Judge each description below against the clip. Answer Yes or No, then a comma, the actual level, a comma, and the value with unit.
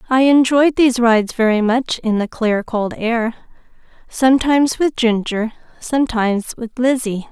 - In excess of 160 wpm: No, average, 140 wpm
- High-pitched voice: Yes, high, 240 Hz